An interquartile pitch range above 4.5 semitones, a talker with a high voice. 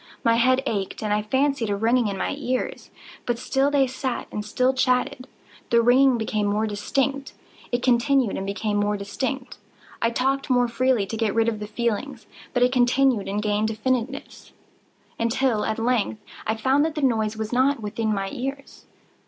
No: average, 3.5 semitones; high, 235 Hz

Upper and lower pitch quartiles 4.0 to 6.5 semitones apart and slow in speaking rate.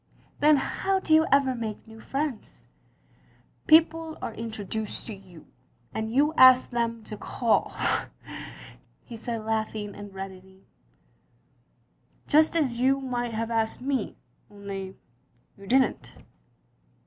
Yes: average, 4.4 semitones; slow, 130 wpm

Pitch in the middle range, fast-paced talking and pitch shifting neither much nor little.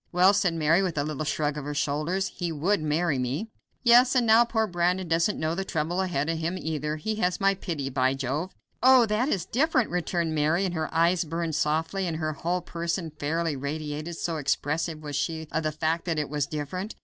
Yes: medium, 165 Hz; fast, 215 wpm; average, 3.4 semitones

